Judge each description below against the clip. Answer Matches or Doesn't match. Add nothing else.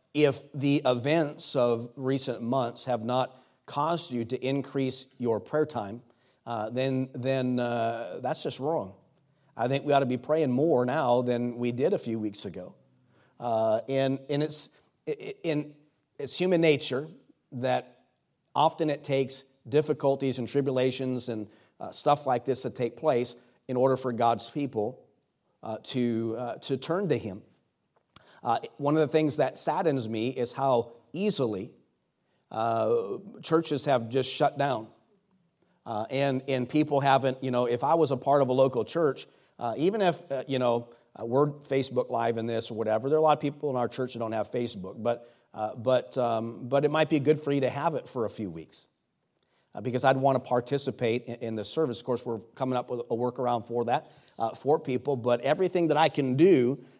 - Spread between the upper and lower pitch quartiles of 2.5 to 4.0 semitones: Matches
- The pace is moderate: Matches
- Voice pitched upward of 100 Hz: Matches